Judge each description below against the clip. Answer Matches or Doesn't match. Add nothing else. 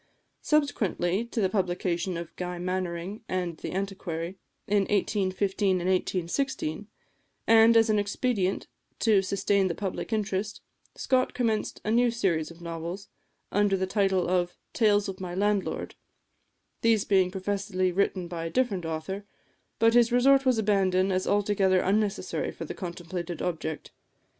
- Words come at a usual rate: Matches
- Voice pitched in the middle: Doesn't match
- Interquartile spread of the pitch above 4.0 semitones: Doesn't match